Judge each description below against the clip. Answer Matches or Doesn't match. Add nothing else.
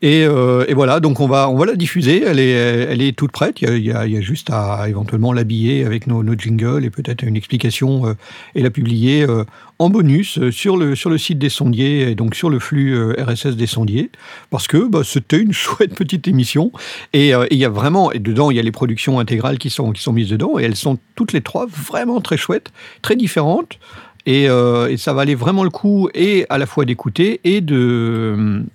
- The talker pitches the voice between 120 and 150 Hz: Matches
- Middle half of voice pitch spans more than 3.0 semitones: Matches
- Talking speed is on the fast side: Matches